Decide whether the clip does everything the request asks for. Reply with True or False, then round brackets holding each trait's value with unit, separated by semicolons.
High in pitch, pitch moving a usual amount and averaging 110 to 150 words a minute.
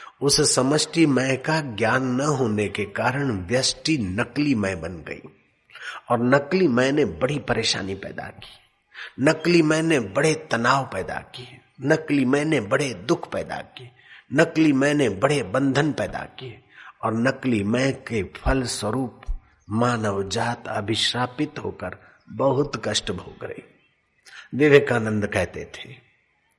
False (130 Hz; 4.3 semitones; 130 wpm)